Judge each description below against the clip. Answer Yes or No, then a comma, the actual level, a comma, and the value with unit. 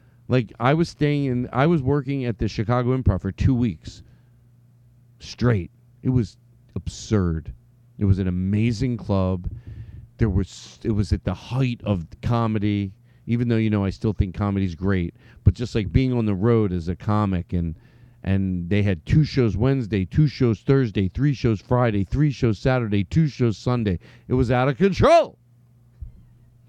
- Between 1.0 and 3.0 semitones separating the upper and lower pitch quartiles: No, average, 3.8 semitones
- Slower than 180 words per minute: Yes, average, 170 wpm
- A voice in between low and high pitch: No, low, 115 Hz